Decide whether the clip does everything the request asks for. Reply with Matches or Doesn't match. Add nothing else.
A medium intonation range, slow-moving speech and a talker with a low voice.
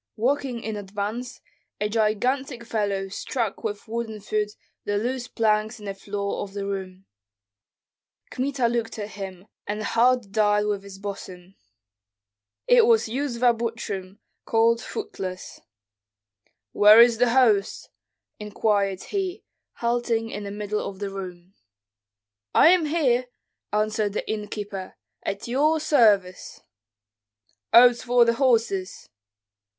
Doesn't match